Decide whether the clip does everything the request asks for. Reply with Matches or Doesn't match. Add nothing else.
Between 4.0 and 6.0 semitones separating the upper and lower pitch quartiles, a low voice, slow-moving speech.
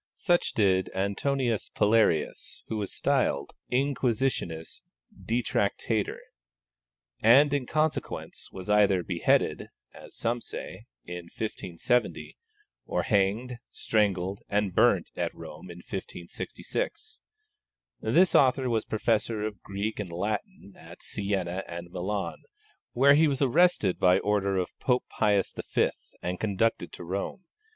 Matches